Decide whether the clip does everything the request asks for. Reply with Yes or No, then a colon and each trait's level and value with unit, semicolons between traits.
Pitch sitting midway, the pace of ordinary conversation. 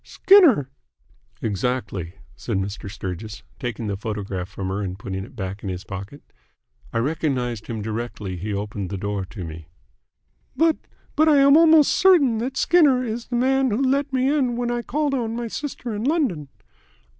No: low, 125 Hz; average, 175 wpm